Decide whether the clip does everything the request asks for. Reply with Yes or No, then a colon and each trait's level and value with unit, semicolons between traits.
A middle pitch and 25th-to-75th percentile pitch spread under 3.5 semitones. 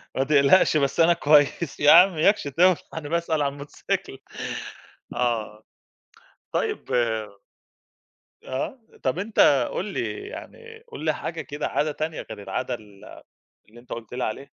No: medium, 145 Hz; wide, 5.6 semitones